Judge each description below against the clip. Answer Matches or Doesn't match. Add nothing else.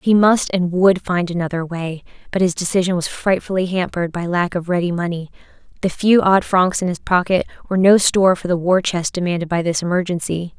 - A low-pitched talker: Doesn't match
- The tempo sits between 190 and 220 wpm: Matches